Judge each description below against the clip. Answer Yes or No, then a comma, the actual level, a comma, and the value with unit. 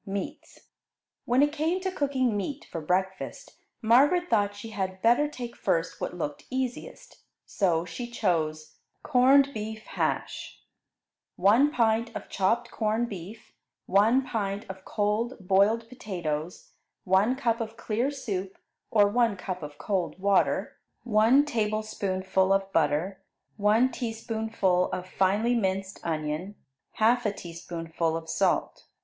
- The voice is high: Yes, high, 210 Hz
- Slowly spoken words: Yes, slow, 130 wpm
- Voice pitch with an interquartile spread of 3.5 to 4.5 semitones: Yes, average, 4.2 semitones